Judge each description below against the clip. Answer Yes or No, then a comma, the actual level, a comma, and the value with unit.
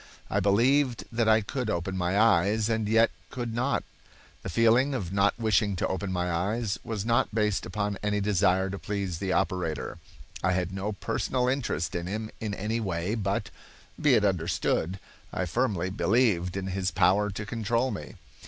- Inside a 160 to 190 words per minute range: Yes, average, 175 wpm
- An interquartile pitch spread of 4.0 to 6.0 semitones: No, average, 3.3 semitones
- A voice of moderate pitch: No, low, 100 Hz